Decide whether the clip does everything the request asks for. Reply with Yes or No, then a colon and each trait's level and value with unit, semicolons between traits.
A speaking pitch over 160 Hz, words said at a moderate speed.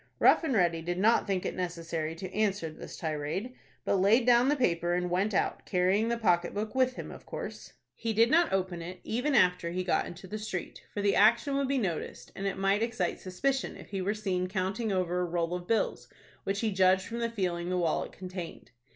No: high, 190 Hz; fast, 220 wpm